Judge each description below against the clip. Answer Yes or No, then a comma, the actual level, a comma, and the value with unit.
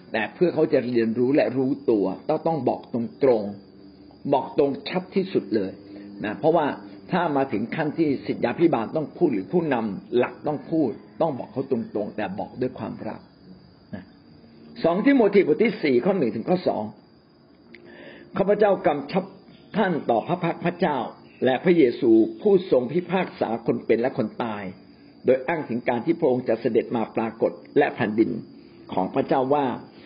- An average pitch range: No, wide, 8.1 semitones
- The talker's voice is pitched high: No, low, 135 Hz